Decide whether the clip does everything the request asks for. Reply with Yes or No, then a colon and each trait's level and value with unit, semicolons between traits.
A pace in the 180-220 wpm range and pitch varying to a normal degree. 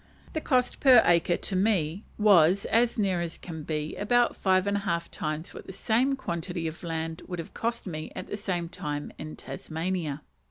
Yes: average, 195 wpm; average, 4.4 semitones